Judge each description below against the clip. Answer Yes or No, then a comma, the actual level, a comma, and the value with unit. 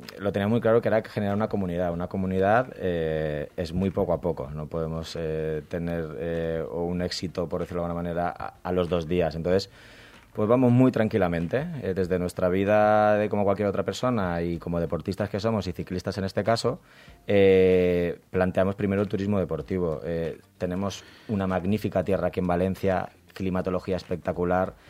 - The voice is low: Yes, very low, 95 Hz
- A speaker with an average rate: Yes, average, 180 wpm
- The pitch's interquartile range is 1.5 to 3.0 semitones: Yes, average, 2.7 semitones